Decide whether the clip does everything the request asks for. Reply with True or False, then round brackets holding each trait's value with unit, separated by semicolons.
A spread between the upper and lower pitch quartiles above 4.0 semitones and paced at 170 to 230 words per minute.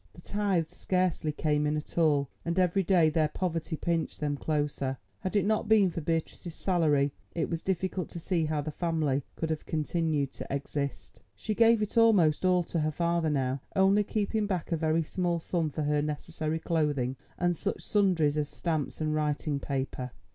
False (3.4 semitones; 185 wpm)